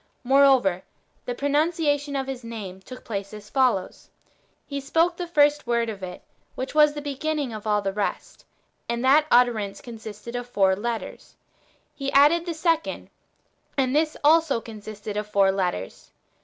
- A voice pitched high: Yes, high, 245 Hz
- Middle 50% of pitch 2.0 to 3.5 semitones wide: No, wide, 5.6 semitones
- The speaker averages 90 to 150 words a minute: No, average, 165 wpm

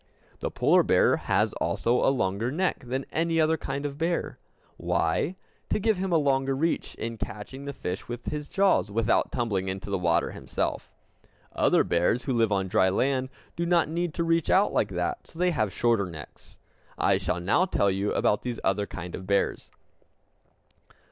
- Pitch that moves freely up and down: Yes, wide, 8.5 semitones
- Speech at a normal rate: Yes, average, 190 wpm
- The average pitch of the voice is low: Yes, low, 125 Hz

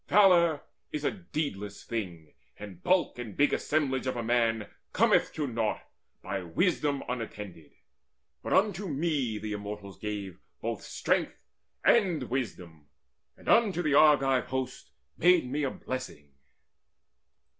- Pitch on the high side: No, low, 130 Hz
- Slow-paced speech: Yes, slow, 130 wpm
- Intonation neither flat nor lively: No, wide, 6.9 semitones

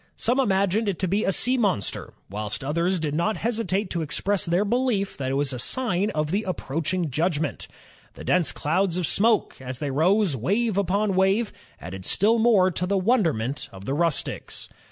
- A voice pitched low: No, medium, 185 Hz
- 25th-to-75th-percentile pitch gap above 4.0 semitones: Yes, wide, 5.6 semitones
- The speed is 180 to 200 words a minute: Yes, average, 185 wpm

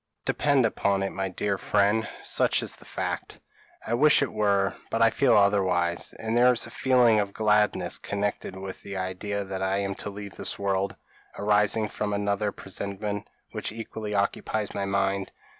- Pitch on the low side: Yes, low, 100 Hz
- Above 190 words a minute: No, average, 175 wpm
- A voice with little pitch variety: Yes, narrow, 1.8 semitones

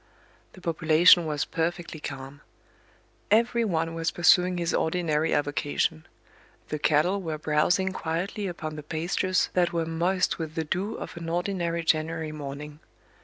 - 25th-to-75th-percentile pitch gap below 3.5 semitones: Yes, narrow, 2.5 semitones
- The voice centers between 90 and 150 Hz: No, medium, 165 Hz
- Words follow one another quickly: No, average, 140 wpm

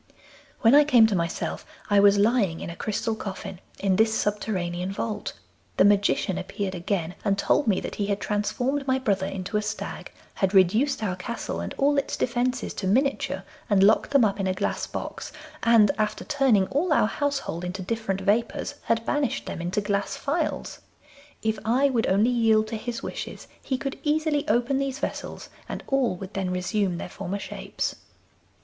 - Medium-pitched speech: No, high, 215 Hz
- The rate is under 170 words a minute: No, average, 180 wpm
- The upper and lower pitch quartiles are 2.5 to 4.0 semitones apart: No, average, 4.5 semitones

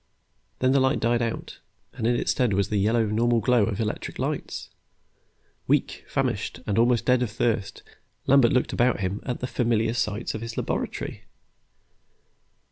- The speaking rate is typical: Yes, average, 165 wpm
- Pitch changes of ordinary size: No, narrow, 2.2 semitones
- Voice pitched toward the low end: Yes, low, 115 Hz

